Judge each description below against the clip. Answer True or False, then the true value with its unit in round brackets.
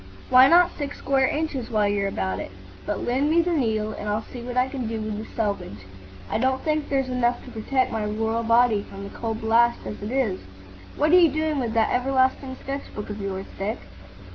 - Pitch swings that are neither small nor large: True (4.0 semitones)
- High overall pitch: True (235 Hz)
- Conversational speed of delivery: False (220 wpm)